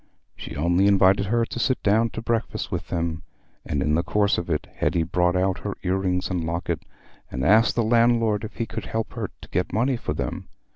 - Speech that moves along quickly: Yes, fast, 220 wpm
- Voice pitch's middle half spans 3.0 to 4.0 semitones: No, average, 4.5 semitones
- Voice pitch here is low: Yes, very low, 95 Hz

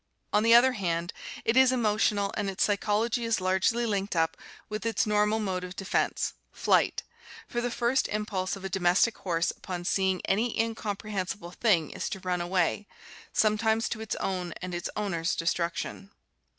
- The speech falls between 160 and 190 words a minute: Yes, average, 175 wpm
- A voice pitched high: Yes, high, 200 Hz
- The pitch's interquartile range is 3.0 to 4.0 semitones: Yes, average, 3.3 semitones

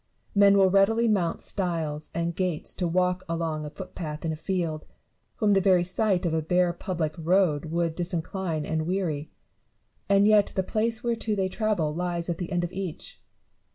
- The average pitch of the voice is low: No, medium, 180 Hz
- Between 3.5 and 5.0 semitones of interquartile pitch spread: No, average, 3.1 semitones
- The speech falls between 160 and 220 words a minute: Yes, average, 180 wpm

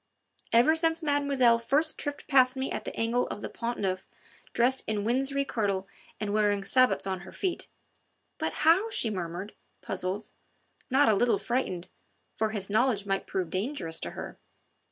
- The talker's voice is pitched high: Yes, high, 230 Hz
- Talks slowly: No, average, 165 wpm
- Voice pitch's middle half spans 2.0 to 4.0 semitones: No, wide, 5.5 semitones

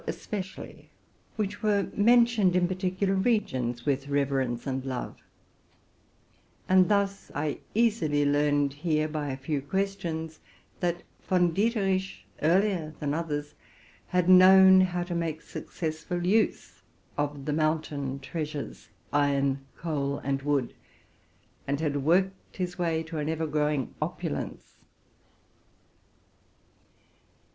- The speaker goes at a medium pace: No, slow, 115 wpm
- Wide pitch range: No, average, 4.5 semitones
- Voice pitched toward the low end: No, medium, 160 Hz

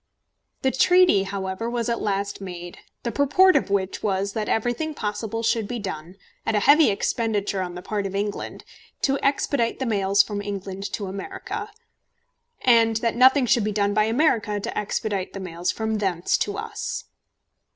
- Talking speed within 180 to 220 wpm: No, average, 170 wpm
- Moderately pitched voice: No, high, 210 Hz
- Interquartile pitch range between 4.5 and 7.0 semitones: No, average, 3.3 semitones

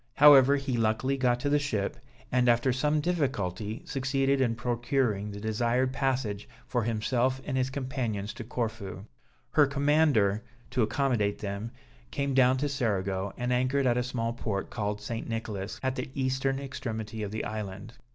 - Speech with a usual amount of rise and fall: Yes, average, 3.8 semitones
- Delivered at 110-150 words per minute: No, average, 160 wpm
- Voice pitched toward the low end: Yes, low, 120 Hz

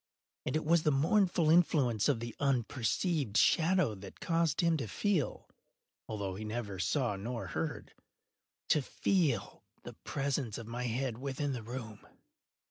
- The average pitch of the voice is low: Yes, low, 130 Hz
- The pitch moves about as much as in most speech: No, wide, 5.7 semitones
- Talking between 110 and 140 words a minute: Yes, slow, 135 wpm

